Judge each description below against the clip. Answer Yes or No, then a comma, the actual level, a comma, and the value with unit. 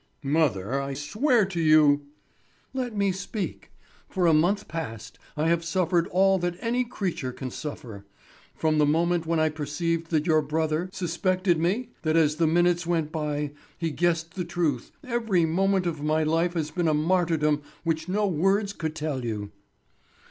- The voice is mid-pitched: Yes, medium, 165 Hz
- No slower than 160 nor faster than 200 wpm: Yes, average, 175 wpm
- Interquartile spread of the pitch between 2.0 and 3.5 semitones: Yes, average, 3.2 semitones